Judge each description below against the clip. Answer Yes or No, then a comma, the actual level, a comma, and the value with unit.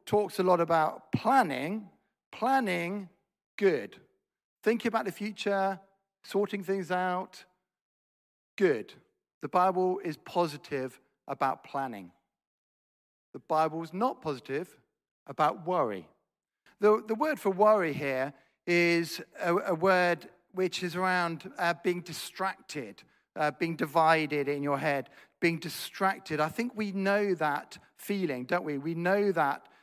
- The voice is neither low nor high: Yes, medium, 180 Hz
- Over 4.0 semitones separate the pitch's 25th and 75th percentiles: No, average, 3.3 semitones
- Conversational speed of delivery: No, slow, 125 wpm